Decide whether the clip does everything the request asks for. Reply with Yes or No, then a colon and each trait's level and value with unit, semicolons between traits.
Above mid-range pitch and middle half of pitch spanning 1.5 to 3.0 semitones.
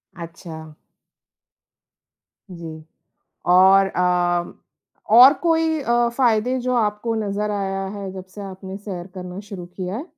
No: high, 195 Hz; average, 3.5 semitones